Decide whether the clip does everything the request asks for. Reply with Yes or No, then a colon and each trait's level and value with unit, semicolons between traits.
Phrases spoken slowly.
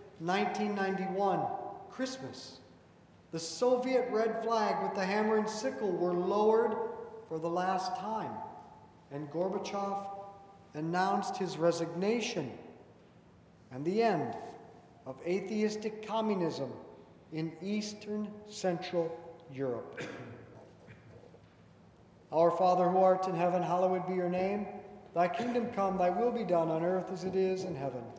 Yes: slow, 120 wpm